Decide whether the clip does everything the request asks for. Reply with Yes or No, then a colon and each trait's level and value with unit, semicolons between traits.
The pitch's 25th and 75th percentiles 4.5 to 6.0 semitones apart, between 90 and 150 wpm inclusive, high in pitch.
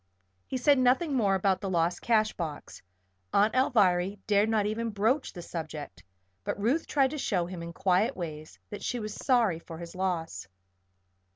No: average, 5.2 semitones; average, 175 wpm; high, 200 Hz